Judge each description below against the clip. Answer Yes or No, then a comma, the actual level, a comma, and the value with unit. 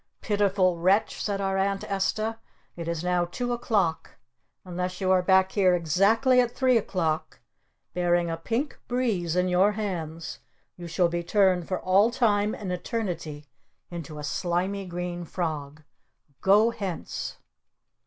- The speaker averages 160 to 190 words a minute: No, average, 145 wpm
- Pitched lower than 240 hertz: Yes, medium, 185 Hz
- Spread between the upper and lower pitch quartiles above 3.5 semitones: No, average, 3.0 semitones